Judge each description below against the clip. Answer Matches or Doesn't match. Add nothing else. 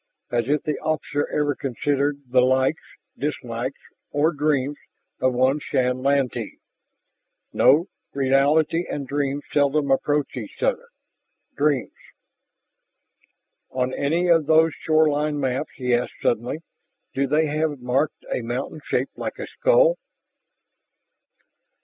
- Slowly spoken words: Matches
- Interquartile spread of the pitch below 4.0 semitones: Matches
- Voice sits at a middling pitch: Matches